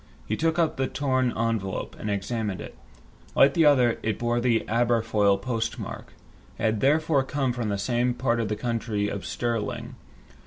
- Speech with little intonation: No, average, 3.2 semitones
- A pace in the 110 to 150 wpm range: No, average, 170 wpm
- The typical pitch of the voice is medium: No, low, 120 Hz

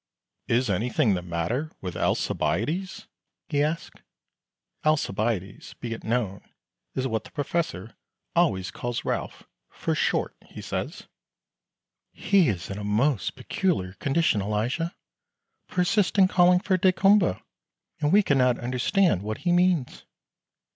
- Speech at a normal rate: No, slow, 125 wpm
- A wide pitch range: Yes, wide, 8.7 semitones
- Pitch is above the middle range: No, low, 130 Hz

